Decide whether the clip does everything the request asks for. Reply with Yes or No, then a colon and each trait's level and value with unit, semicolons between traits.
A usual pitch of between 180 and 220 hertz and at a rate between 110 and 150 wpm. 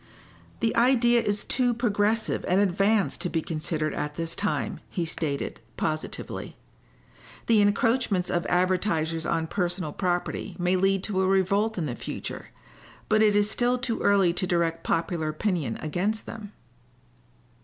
Yes: high, 190 Hz; average, 145 wpm